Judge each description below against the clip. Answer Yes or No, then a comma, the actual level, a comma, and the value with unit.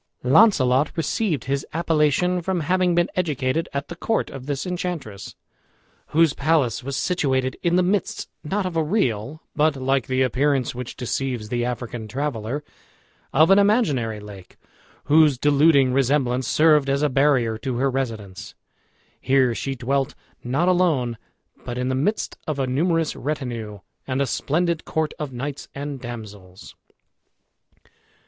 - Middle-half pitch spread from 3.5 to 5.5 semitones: Yes, average, 4.2 semitones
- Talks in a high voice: No, medium, 140 Hz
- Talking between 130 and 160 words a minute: Yes, average, 145 wpm